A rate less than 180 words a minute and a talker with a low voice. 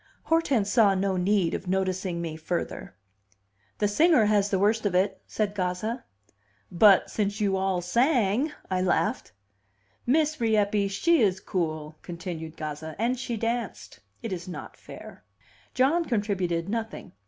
No: average, 140 wpm; high, 200 Hz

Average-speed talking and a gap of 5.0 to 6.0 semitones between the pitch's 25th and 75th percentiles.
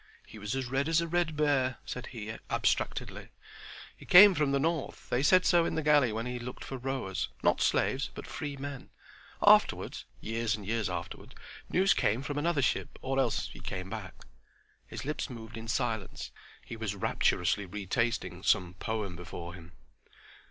Yes: average, 165 wpm; wide, 5.4 semitones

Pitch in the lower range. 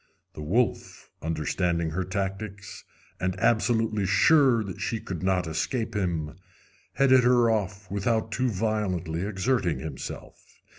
Yes: low, 100 Hz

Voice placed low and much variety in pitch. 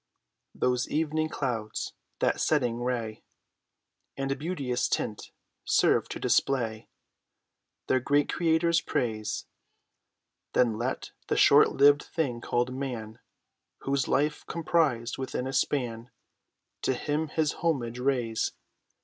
No: low, 130 Hz; average, 3.8 semitones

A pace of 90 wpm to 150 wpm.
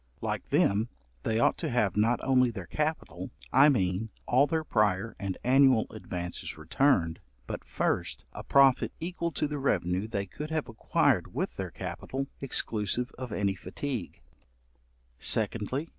Yes: average, 145 wpm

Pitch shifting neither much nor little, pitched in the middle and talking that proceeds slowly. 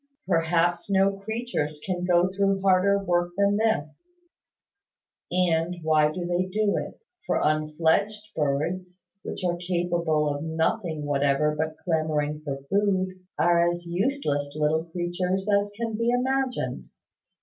Yes: average, 3.9 semitones; medium, 175 Hz; slow, 130 wpm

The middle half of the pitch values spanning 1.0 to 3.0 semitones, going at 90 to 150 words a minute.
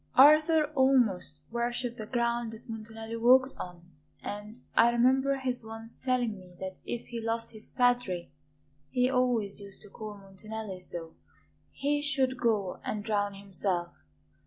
No: average, 3.7 semitones; average, 145 wpm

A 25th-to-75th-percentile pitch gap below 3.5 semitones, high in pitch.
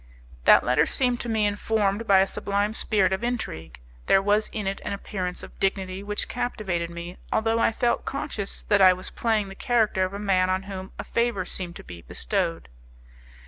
Yes: average, 2.9 semitones; high, 200 Hz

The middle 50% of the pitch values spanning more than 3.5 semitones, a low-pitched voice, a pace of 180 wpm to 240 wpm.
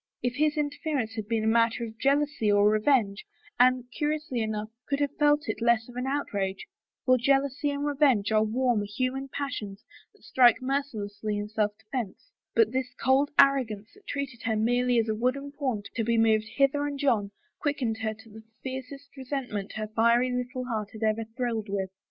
No: average, 4.1 semitones; high, 245 Hz; average, 185 wpm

